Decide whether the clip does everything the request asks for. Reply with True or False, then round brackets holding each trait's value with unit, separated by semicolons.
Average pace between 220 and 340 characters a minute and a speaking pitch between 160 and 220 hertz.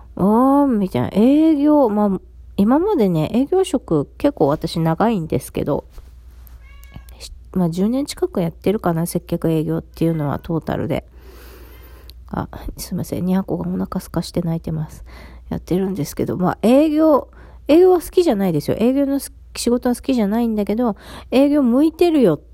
True (320 characters per minute; 190 Hz)